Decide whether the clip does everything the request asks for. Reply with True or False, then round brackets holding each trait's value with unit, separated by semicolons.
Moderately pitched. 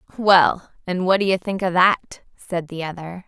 True (180 Hz)